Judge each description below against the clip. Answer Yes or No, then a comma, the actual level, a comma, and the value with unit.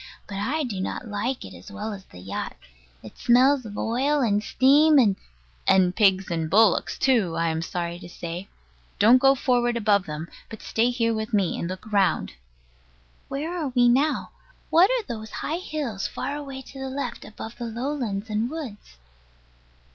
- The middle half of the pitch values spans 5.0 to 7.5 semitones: Yes, wide, 5.4 semitones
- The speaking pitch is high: Yes, high, 225 Hz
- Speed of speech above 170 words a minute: Yes, average, 180 wpm